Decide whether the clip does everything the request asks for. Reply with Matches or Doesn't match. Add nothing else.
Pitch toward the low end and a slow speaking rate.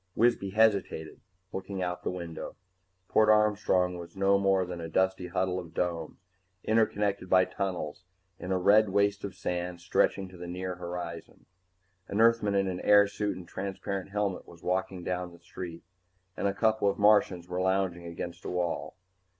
Doesn't match